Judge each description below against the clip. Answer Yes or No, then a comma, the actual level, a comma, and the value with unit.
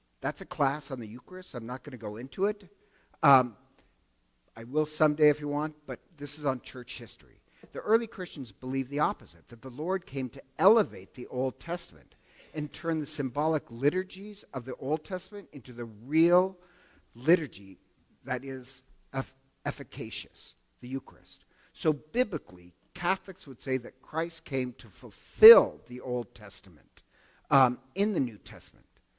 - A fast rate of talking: No, average, 160 wpm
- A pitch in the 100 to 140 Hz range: Yes, low, 135 Hz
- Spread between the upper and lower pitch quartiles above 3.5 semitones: Yes, average, 5.1 semitones